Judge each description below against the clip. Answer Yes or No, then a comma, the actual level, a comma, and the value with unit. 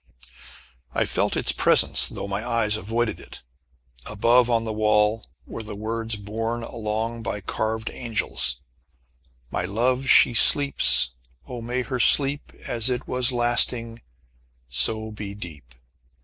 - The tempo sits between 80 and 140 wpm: Yes, slow, 135 wpm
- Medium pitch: No, low, 115 Hz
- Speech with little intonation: Yes, narrow, 2.2 semitones